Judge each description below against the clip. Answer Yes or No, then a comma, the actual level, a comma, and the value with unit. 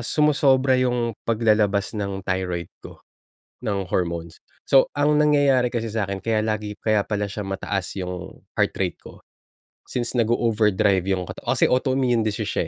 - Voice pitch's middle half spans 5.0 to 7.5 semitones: No, average, 4.1 semitones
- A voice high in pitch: No, low, 110 Hz